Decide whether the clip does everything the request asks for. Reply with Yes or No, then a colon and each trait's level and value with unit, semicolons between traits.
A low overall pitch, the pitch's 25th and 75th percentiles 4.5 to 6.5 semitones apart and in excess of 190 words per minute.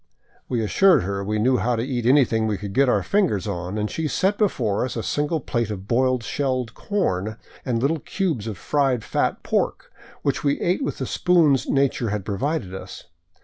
Yes: low, 120 Hz; wide, 5.5 semitones; average, 200 wpm